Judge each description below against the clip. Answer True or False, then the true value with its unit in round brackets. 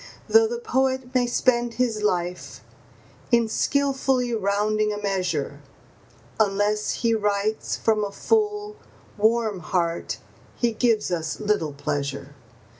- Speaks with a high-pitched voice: True (215 Hz)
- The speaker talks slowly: True (115 wpm)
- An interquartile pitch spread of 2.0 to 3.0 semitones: False (3.9 semitones)